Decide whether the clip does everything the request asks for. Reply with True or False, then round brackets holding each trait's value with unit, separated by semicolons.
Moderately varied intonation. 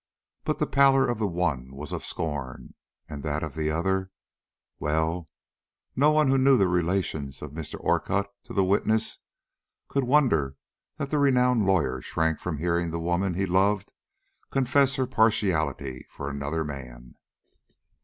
False (7.1 semitones)